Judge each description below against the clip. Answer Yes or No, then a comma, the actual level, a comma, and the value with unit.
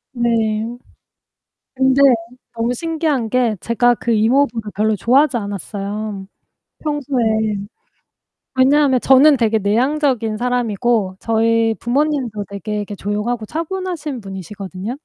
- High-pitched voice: Yes, high, 235 Hz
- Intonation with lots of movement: No, average, 4.0 semitones